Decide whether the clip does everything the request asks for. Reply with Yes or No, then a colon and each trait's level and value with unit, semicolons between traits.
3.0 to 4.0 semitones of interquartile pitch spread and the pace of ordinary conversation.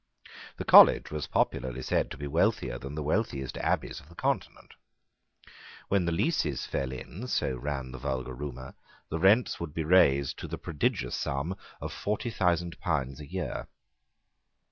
No: average, 4.7 semitones; average, 165 wpm